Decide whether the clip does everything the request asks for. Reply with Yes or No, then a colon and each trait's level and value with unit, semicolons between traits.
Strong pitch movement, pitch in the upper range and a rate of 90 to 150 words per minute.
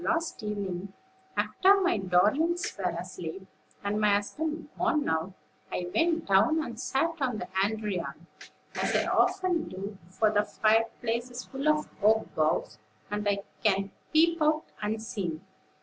Yes: wide, 7.9 semitones; high, 215 Hz; average, 145 wpm